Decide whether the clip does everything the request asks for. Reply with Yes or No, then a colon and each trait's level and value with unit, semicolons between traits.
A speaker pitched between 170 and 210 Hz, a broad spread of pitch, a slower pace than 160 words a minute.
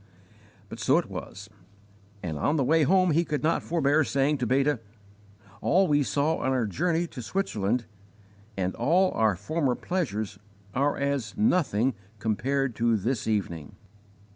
No: low, 135 Hz; wide, 6.3 semitones; average, 150 wpm